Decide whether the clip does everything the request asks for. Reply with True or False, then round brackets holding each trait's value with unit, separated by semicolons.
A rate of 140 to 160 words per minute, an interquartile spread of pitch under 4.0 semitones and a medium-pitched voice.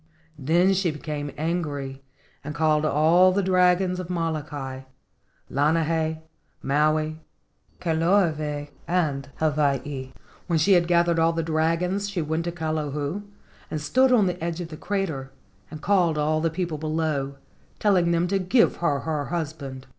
True (145 wpm; 2.8 semitones; 160 Hz)